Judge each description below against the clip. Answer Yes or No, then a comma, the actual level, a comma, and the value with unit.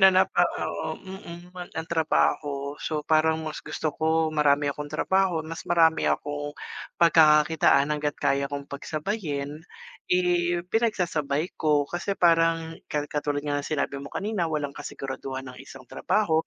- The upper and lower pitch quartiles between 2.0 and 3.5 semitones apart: Yes, average, 2.9 semitones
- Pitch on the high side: No, medium, 155 Hz